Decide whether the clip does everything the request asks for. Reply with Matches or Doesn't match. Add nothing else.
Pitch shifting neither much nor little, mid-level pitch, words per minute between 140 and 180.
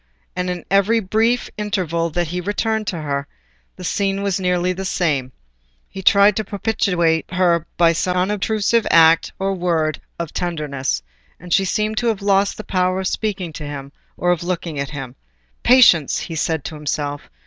Matches